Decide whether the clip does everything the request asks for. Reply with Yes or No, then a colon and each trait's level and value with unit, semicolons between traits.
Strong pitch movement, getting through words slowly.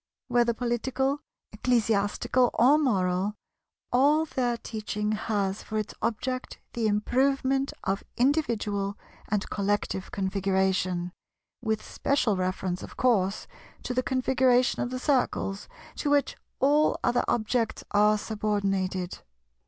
No: average, 4.2 semitones; slow, 110 wpm